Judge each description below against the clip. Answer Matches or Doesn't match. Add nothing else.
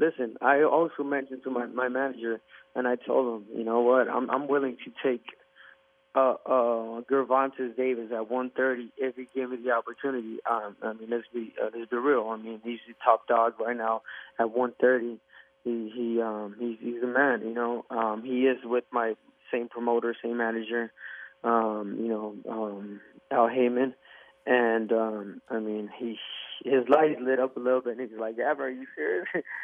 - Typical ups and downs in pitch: Doesn't match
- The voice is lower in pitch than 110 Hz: Doesn't match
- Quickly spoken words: Doesn't match